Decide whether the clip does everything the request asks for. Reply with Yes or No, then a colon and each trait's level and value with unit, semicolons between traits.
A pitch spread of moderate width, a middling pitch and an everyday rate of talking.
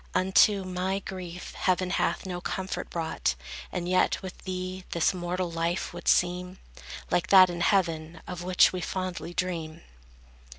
No: narrow, 1.2 semitones; medium, 180 Hz; average, 145 wpm